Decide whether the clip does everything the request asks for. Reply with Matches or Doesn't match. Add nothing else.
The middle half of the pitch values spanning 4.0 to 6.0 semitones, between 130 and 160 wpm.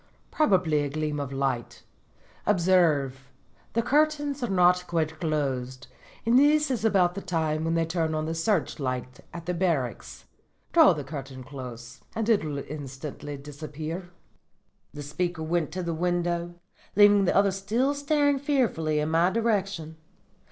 Matches